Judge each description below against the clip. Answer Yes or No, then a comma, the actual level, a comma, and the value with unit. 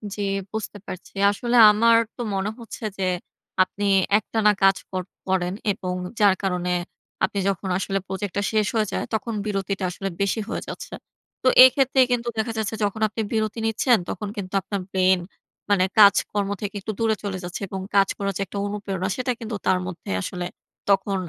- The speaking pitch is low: No, high, 200 Hz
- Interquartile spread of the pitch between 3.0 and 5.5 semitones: No, narrow, 2.4 semitones